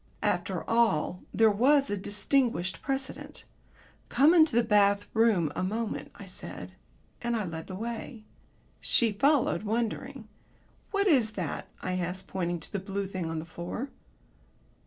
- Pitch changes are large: No, average, 4.3 semitones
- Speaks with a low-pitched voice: No, high, 215 Hz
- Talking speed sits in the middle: Yes, average, 150 wpm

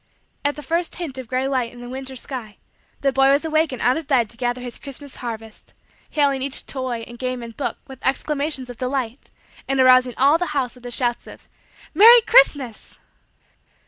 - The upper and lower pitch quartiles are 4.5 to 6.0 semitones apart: No, average, 2.7 semitones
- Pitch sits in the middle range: No, very high, 260 Hz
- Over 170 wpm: Yes, average, 200 wpm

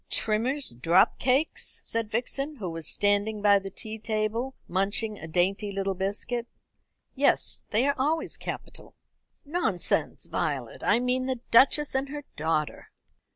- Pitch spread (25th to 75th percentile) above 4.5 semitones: Yes, average, 5.0 semitones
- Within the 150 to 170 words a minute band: No, average, 140 wpm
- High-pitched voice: Yes, high, 220 Hz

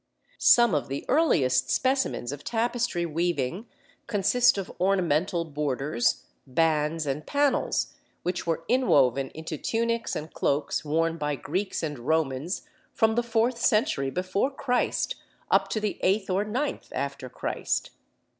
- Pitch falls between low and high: Yes, medium, 170 Hz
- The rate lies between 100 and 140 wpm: Yes, slow, 135 wpm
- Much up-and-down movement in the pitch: Yes, wide, 7.5 semitones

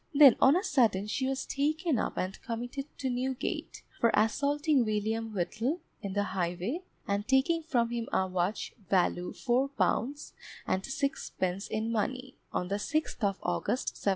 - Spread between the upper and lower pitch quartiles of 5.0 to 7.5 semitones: Yes, wide, 5.4 semitones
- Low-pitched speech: No, high, 235 Hz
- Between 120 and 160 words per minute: Yes, average, 155 wpm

